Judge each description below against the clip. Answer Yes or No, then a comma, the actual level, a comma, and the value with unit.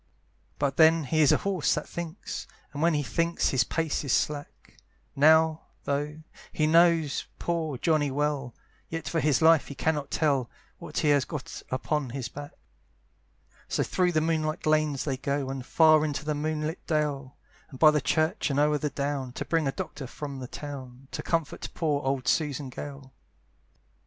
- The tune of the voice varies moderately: No, narrow, 2.3 semitones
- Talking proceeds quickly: No, average, 175 wpm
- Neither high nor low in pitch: Yes, medium, 150 Hz